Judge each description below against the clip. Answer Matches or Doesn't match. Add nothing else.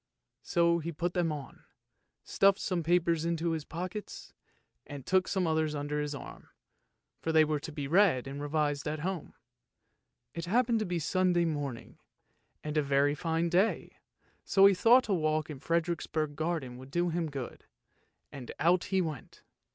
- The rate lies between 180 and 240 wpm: Doesn't match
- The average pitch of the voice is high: Doesn't match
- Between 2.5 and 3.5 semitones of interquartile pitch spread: Matches